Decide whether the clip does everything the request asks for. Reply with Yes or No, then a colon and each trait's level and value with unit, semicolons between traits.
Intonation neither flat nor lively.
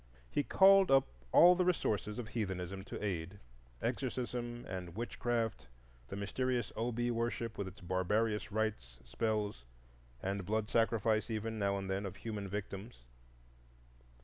Yes: average, 3.5 semitones